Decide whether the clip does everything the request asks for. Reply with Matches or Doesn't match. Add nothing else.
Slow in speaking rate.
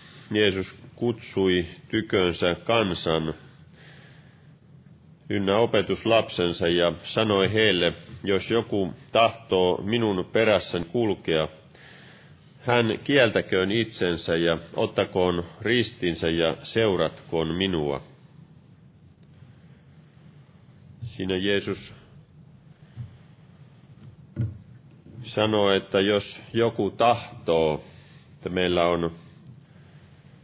Matches